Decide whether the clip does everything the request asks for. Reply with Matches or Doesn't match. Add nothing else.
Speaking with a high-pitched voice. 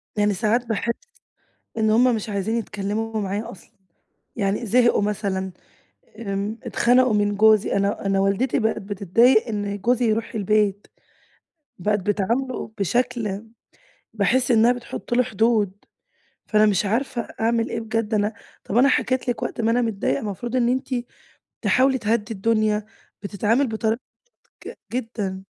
Matches